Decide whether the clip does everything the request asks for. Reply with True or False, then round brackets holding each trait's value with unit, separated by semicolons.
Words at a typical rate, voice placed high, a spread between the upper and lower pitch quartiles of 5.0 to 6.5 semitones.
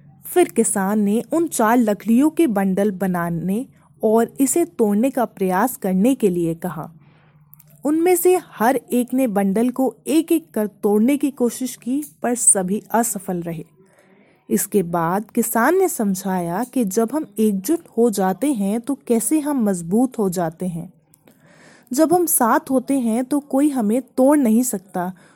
True (160 wpm; 225 Hz; 5.4 semitones)